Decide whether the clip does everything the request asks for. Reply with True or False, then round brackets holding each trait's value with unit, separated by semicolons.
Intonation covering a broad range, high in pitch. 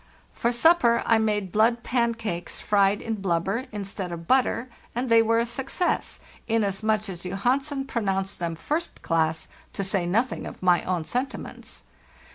False (4.0 semitones; 220 Hz)